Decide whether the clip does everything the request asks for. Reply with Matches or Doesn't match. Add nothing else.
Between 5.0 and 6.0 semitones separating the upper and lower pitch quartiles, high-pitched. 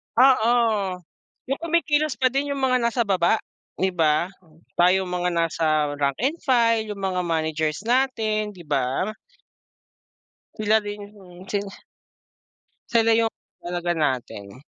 Matches